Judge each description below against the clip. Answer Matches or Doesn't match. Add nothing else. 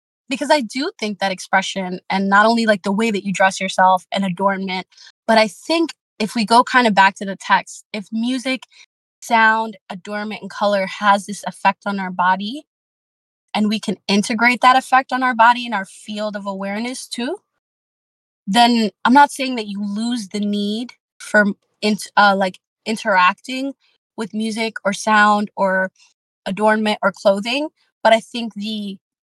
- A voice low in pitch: Doesn't match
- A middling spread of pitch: Matches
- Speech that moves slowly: Doesn't match